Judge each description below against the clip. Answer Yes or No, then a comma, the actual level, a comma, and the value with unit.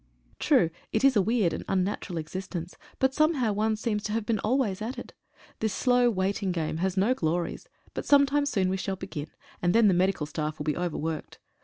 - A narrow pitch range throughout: No, average, 4.9 semitones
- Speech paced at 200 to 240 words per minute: Yes, fast, 205 wpm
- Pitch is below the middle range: No, high, 195 Hz